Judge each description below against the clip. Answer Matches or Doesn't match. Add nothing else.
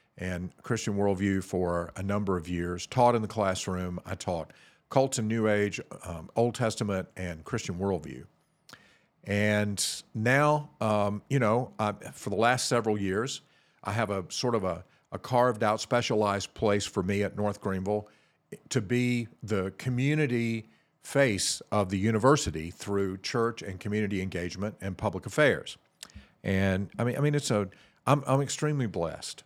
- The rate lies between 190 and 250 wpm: Doesn't match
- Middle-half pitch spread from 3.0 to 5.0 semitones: Matches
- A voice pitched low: Matches